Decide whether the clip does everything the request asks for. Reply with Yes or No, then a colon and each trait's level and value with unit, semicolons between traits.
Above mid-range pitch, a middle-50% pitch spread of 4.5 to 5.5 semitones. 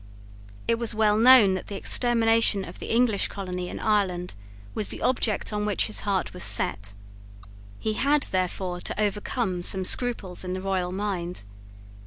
No: high, 200 Hz; average, 3.5 semitones